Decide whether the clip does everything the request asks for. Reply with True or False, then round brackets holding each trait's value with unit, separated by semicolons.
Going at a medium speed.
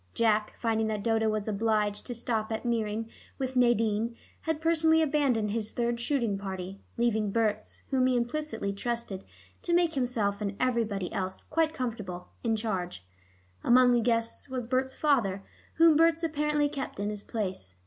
True (160 wpm)